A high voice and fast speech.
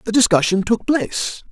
No: high, 215 Hz; average, 160 wpm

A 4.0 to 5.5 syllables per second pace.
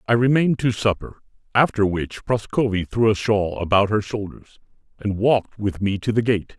Yes: 5.1 syllables/s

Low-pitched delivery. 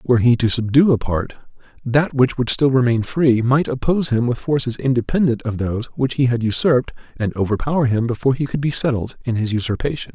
Yes: low, 125 Hz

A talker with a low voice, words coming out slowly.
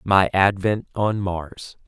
Yes: very low, 95 Hz; slow, 130 wpm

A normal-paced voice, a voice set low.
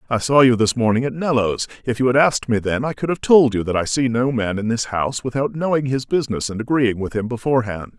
No: fast, 265 wpm; low, 125 Hz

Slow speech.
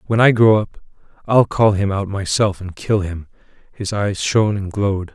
No: average, 200 wpm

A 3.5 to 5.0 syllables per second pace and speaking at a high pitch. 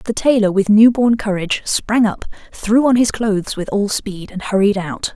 Yes: 4.9 syllables/s; high, 210 Hz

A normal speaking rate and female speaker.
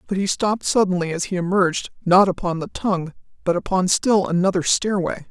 Yes: average, 180 wpm; female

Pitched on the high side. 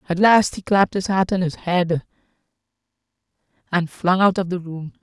No: medium, 180 Hz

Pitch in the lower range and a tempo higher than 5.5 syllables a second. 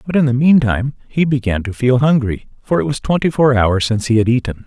Yes: low, 125 Hz; 6.1 syllables/s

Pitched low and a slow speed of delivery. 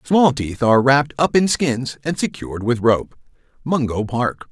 No: low, 130 Hz; average, 175 wpm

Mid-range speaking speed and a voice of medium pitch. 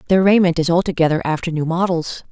Yes: average, 180 wpm; medium, 170 Hz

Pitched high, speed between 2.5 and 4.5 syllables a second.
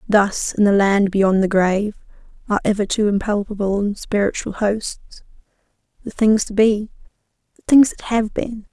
No: high, 205 Hz; 5.0 syllables/s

